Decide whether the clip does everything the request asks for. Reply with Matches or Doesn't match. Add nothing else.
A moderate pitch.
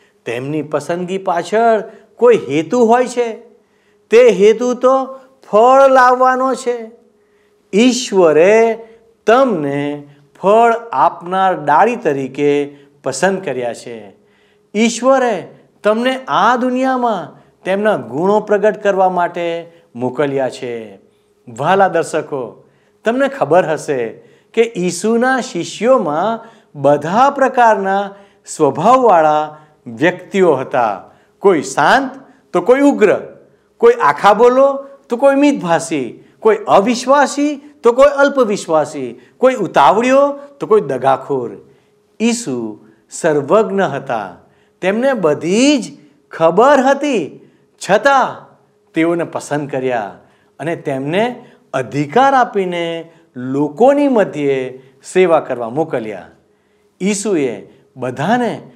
Doesn't match